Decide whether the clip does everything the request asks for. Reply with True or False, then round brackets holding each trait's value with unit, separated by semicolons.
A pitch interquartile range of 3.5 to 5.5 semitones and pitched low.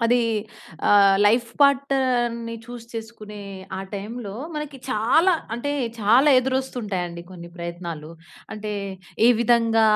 False (3.8 semitones; 230 Hz)